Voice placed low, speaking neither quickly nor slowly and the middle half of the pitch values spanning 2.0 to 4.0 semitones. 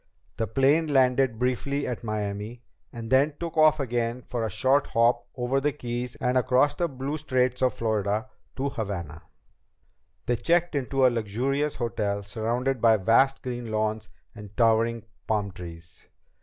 Yes: low, 120 Hz; average, 155 wpm; average, 3.6 semitones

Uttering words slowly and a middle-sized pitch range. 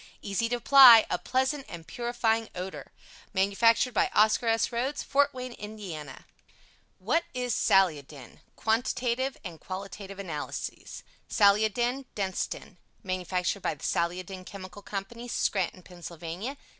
Yes: slow, 120 wpm; average, 4.6 semitones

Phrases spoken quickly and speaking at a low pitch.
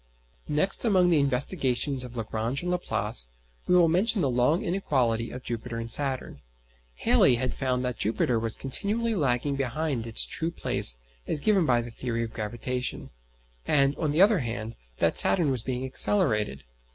No: average, 165 wpm; low, 130 Hz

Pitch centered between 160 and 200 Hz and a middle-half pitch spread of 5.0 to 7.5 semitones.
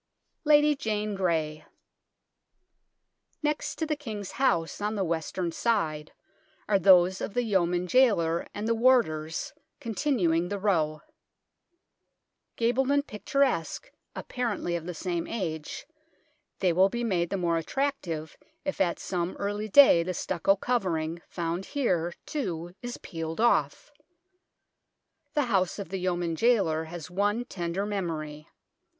Yes: high, 190 Hz; wide, 5.5 semitones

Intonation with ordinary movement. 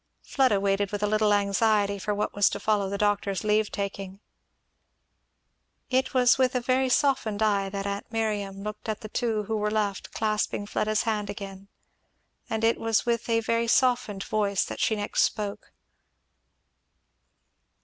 No: narrow, 2.0 semitones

